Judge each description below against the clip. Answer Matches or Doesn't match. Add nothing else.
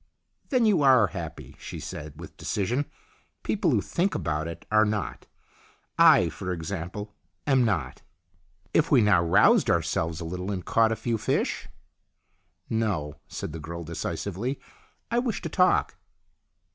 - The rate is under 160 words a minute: Doesn't match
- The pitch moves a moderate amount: Doesn't match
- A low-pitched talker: Matches